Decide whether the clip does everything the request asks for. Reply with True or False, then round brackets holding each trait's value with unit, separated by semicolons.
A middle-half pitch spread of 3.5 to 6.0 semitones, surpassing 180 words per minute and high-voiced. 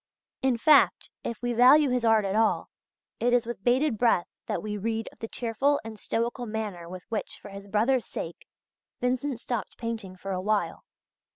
False (2.9 semitones; 195 wpm; 225 Hz)